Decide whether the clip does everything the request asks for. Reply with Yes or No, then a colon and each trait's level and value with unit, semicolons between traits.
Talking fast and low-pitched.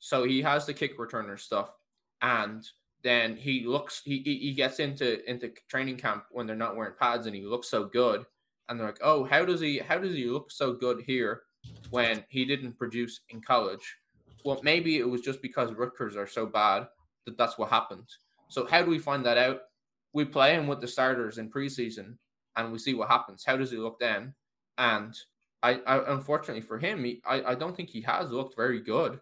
Yes: fast, 210 wpm; low, 125 Hz